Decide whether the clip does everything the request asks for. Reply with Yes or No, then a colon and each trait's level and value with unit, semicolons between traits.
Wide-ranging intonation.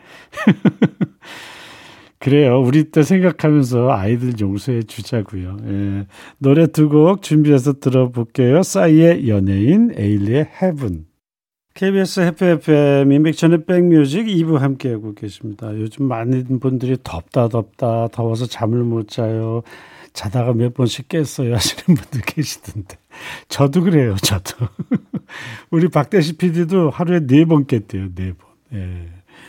Yes: wide, 5.8 semitones